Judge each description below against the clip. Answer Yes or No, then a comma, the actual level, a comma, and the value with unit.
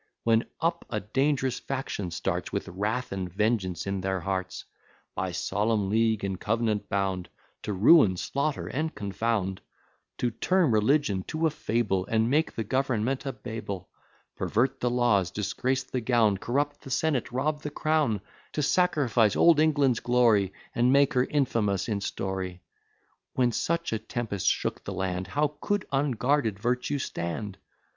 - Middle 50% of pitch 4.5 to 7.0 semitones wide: Yes, wide, 5.5 semitones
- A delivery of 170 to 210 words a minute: No, average, 150 wpm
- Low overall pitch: Yes, low, 115 Hz